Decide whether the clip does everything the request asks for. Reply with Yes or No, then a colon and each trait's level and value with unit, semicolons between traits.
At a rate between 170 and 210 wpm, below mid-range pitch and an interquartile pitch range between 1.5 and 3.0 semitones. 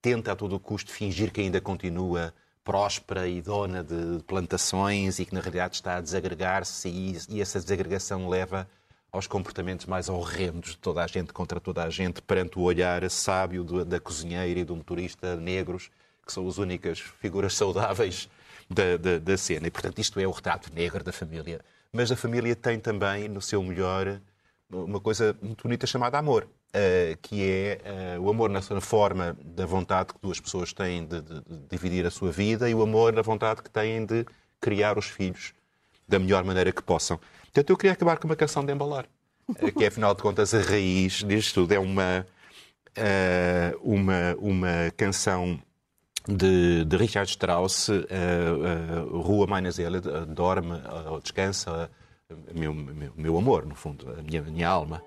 Yes: average, 180 wpm; very low, 95 Hz; narrow, 2.6 semitones